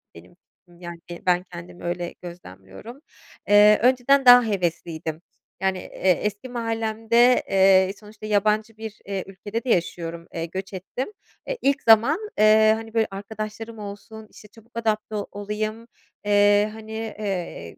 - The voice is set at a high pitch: Yes, high, 210 Hz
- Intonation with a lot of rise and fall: No, average, 3.4 semitones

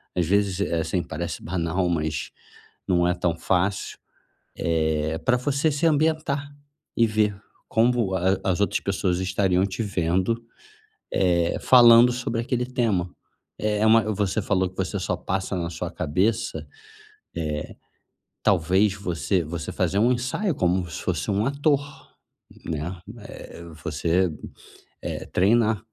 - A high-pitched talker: No, very low, 95 Hz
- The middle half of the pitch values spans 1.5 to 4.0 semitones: No, average, 4.8 semitones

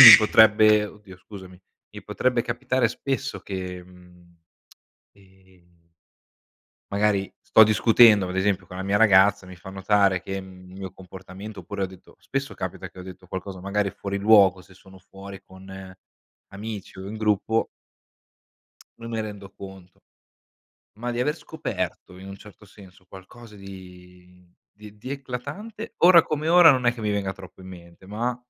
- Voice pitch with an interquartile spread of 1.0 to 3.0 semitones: Yes, average, 2.7 semitones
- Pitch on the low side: Yes, low, 100 Hz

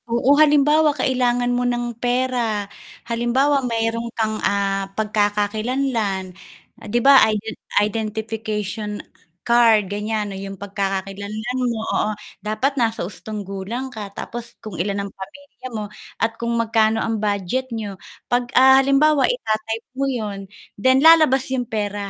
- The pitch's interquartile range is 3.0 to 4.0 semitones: Yes, average, 3.3 semitones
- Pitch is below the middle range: No, high, 225 Hz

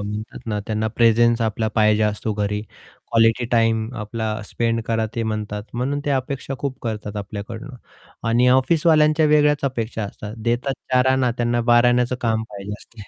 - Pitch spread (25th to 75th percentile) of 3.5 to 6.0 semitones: No, average, 2.7 semitones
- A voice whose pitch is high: No, low, 115 Hz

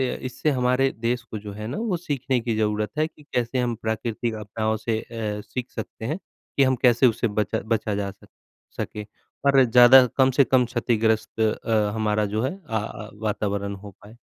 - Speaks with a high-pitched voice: No, low, 115 Hz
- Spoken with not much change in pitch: No, average, 3.0 semitones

